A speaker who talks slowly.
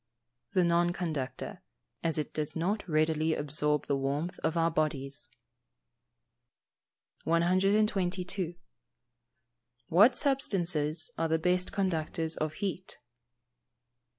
Yes: slow, 100 wpm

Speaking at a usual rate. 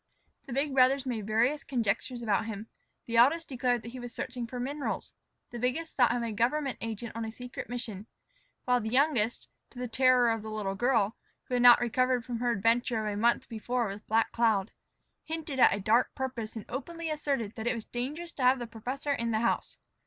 No: fast, 210 wpm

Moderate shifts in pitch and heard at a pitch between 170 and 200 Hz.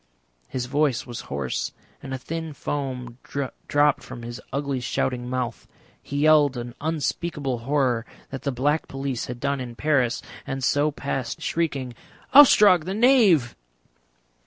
No: average, 3.3 semitones; low, 135 Hz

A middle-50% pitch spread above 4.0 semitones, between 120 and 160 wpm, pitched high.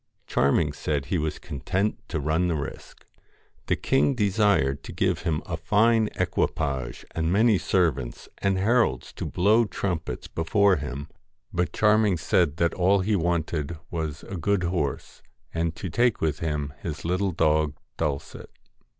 No: average, 4.8 semitones; average, 150 wpm; very low, 85 Hz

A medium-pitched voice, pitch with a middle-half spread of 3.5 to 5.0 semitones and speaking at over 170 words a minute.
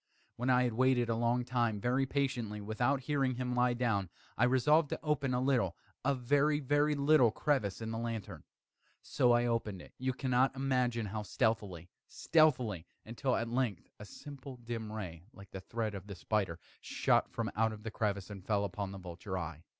No: low, 120 Hz; average, 3.9 semitones; average, 190 wpm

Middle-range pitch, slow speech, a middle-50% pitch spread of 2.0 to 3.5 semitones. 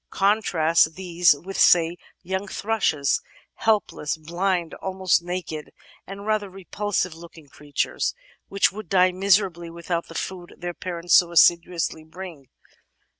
Yes: medium, 175 Hz; slow, 125 wpm; narrow, 2.5 semitones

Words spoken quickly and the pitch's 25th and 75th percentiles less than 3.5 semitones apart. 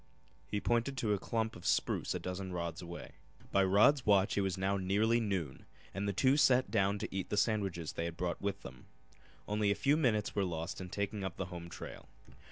Yes: fast, 215 wpm; average, 2.8 semitones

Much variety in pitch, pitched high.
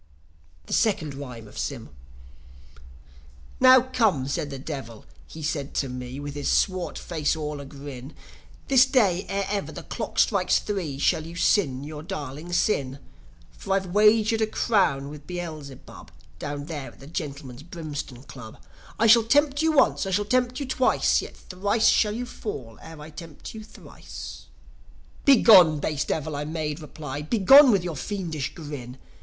No: wide, 6.5 semitones; medium, 160 Hz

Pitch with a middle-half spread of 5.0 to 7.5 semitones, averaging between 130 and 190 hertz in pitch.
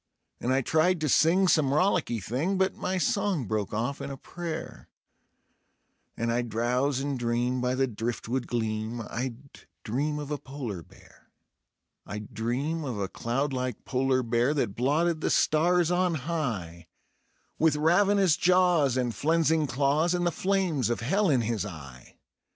Yes: wide, 5.5 semitones; low, 135 Hz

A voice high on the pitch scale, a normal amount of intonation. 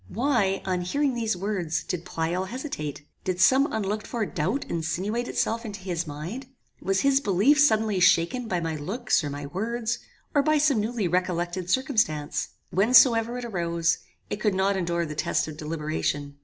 No: high, 195 Hz; wide, 5.8 semitones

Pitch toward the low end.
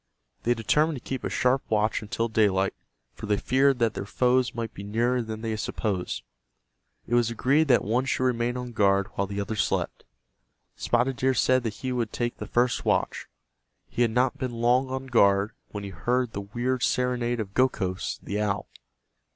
Yes: low, 120 Hz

